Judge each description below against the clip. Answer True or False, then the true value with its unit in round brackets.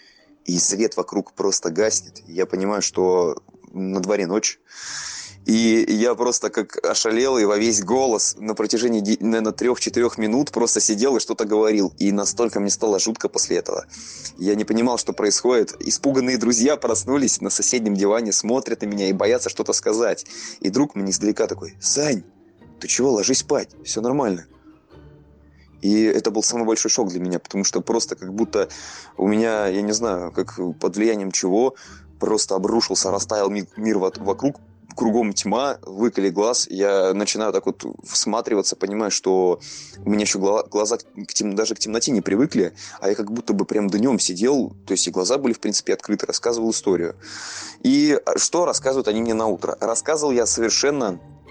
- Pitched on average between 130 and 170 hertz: False (110 Hz)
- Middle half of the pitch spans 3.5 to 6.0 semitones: False (3.1 semitones)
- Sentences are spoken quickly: True (170 wpm)